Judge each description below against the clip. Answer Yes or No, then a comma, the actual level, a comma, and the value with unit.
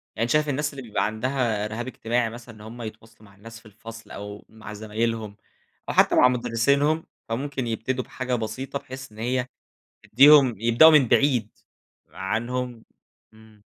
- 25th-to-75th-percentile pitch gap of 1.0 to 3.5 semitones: Yes, average, 2.8 semitones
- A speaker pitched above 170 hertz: No, low, 115 Hz